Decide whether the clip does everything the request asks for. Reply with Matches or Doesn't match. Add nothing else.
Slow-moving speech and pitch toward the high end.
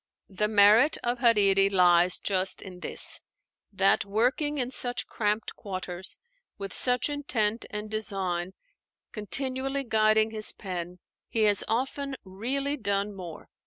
Matches